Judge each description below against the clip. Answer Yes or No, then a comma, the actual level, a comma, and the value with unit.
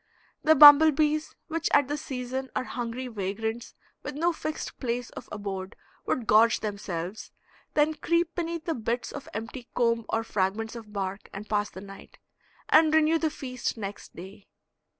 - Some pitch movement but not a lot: No, wide, 6.4 semitones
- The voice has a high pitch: Yes, high, 240 Hz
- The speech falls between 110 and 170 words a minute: Yes, average, 165 wpm